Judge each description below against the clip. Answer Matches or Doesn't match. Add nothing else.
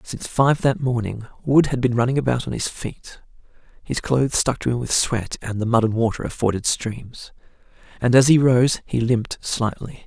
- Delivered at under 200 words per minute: Doesn't match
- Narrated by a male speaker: Matches